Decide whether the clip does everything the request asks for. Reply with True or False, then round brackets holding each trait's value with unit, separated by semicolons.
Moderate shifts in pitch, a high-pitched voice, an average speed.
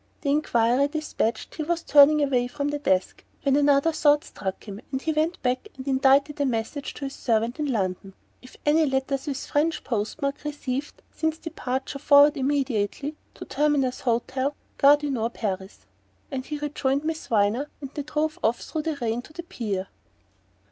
True (3.3 semitones; 275 Hz; 180 wpm)